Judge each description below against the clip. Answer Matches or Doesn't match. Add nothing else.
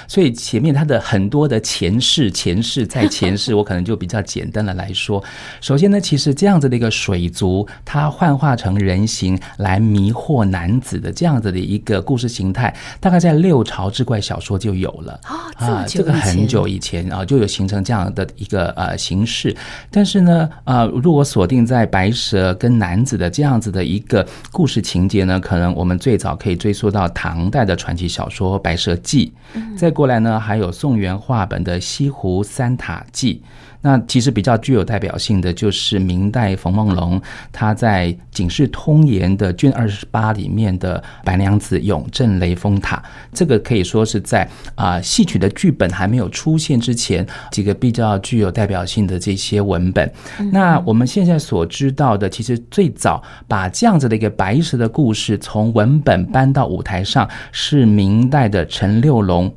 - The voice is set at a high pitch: Doesn't match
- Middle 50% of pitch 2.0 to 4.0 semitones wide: Doesn't match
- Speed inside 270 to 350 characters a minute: Matches